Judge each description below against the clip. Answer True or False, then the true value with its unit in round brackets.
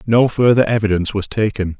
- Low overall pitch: True (105 Hz)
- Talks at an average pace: True (165 wpm)